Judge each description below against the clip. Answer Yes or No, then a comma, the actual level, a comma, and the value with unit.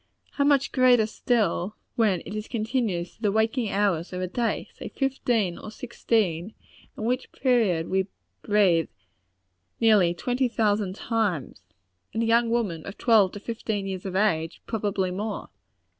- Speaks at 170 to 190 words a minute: No, average, 155 wpm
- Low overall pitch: No, high, 215 Hz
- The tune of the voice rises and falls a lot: No, average, 3.6 semitones